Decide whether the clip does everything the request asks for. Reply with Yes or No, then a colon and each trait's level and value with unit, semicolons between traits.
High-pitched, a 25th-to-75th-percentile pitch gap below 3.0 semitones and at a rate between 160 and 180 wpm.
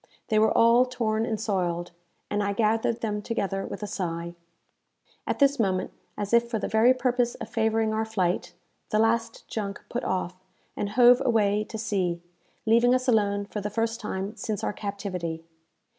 Yes: high, 215 Hz; narrow, 2.6 semitones; average, 175 wpm